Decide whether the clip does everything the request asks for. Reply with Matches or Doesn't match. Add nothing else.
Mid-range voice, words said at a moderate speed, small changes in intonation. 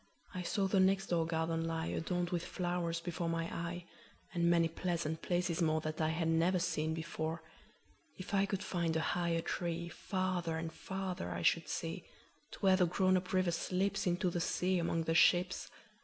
Matches